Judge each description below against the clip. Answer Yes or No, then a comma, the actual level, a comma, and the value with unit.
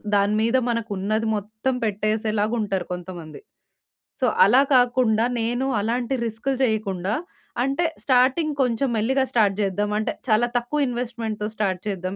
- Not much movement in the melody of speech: No, average, 3.2 semitones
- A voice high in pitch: Yes, high, 220 Hz